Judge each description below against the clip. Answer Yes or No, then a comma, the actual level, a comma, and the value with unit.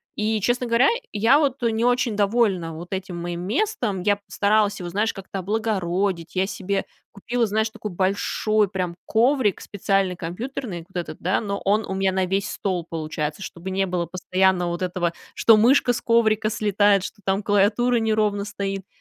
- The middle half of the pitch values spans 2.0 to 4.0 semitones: Yes, average, 3.0 semitones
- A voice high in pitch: Yes, high, 200 Hz